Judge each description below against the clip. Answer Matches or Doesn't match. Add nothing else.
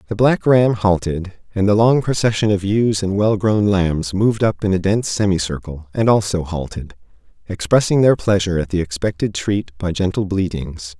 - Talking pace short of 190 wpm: Matches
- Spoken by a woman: Doesn't match